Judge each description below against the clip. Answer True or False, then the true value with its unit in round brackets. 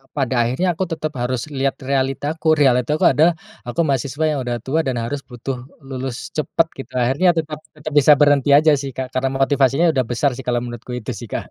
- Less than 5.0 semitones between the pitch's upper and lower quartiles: True (2.9 semitones)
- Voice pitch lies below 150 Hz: True (135 Hz)